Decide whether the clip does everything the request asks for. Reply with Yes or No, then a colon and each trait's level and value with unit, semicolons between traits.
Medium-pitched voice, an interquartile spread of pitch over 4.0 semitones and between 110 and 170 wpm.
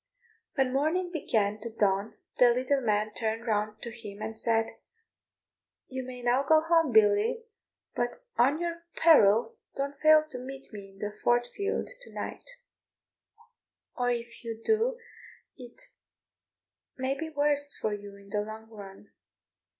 No: high, 240 Hz; average, 5.1 semitones; average, 150 wpm